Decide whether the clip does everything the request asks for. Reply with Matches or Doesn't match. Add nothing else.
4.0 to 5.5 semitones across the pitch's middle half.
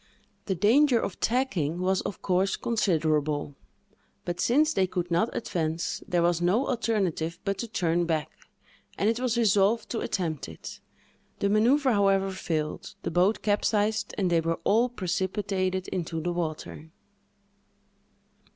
Matches